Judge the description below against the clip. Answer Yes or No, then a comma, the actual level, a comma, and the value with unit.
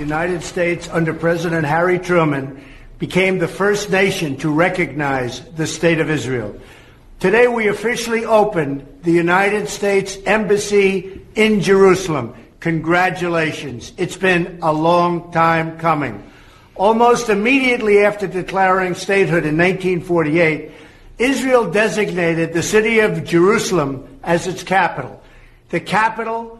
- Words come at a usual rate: No, slow, 115 wpm